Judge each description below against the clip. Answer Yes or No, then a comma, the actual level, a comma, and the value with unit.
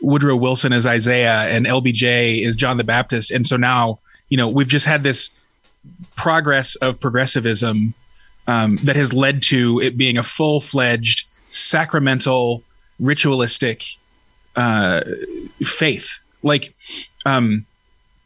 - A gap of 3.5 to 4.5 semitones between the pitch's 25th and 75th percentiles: No, average, 2.9 semitones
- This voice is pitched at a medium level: No, low, 130 Hz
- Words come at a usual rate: No, slow, 125 wpm